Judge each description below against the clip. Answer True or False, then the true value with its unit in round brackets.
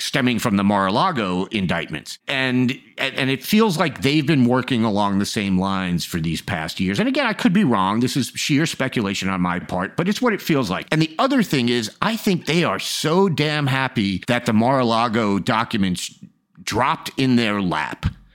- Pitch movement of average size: False (7.8 semitones)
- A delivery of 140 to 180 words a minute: False (195 wpm)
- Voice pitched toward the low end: True (130 Hz)